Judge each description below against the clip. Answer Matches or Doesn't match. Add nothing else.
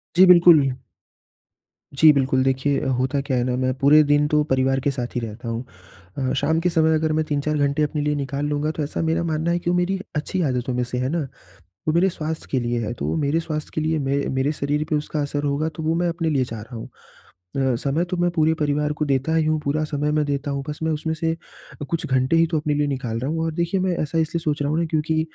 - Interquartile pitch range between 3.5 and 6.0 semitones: Doesn't match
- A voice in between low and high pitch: Matches